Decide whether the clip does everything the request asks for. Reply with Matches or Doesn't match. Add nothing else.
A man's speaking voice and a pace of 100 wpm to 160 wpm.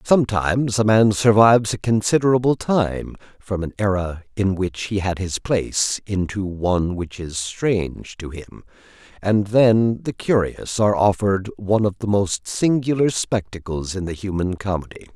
Matches